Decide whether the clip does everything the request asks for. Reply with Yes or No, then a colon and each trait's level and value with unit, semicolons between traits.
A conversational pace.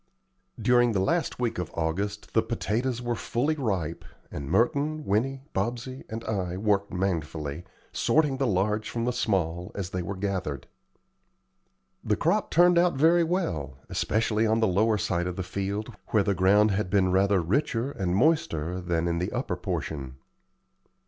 Yes: average, 160 wpm